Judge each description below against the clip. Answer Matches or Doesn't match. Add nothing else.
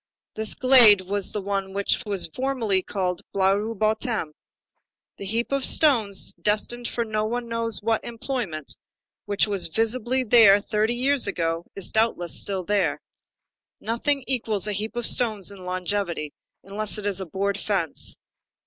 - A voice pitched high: Matches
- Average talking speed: Matches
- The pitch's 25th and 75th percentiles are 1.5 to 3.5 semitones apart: Matches